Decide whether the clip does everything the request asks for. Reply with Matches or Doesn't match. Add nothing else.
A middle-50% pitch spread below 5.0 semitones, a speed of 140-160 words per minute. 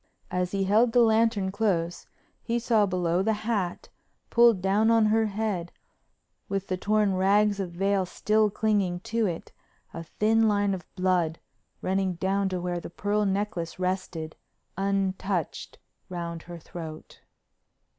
Matches